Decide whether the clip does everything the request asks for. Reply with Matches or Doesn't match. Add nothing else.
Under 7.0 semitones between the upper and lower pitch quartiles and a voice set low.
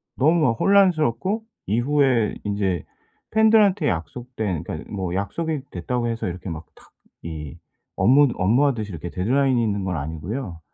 Doesn't match